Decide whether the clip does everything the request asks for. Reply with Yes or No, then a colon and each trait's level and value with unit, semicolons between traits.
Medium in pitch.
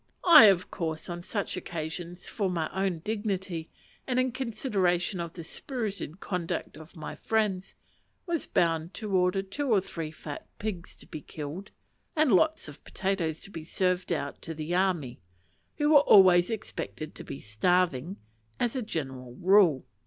Yes: medium, 180 Hz